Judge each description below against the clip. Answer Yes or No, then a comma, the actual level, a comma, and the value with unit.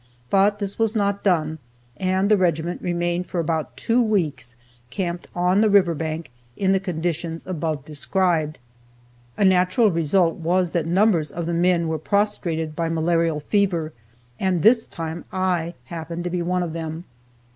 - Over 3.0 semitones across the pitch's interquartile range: No, average, 2.7 semitones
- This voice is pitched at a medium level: Yes, medium, 175 Hz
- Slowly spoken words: No, average, 160 wpm